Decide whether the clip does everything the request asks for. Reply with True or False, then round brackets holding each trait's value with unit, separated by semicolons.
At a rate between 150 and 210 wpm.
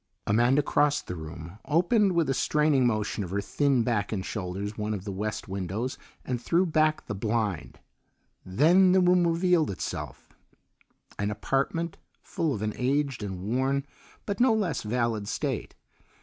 True (160 wpm)